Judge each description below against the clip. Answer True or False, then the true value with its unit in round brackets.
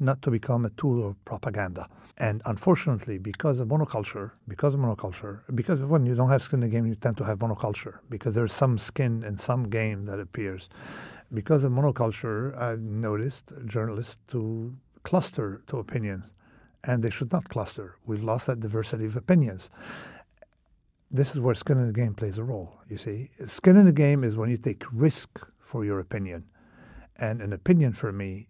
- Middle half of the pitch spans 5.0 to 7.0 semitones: False (4.1 semitones)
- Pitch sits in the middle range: False (115 Hz)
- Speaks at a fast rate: False (185 wpm)